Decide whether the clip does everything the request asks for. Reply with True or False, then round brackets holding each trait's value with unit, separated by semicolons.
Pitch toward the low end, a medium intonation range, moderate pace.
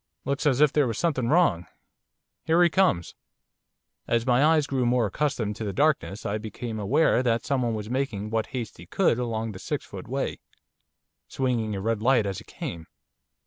True (120 Hz; 4.4 semitones; 185 wpm)